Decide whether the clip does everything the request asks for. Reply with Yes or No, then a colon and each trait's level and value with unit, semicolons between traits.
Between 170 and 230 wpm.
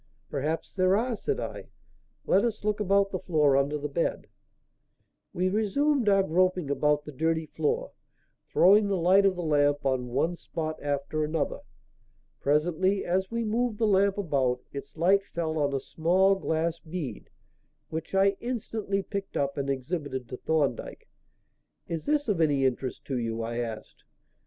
No: average, 160 wpm